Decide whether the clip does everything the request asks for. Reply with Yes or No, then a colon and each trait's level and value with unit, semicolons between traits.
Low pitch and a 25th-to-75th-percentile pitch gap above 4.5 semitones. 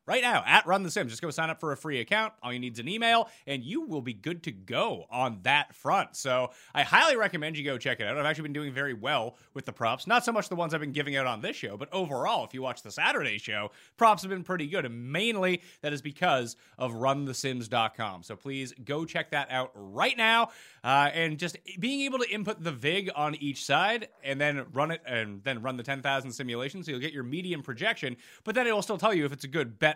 No: medium, 145 Hz; wide, 5.5 semitones